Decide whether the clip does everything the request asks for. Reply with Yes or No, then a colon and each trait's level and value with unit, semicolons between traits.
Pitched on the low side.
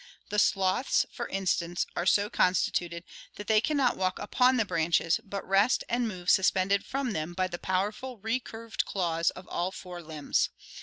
No: high, 190 Hz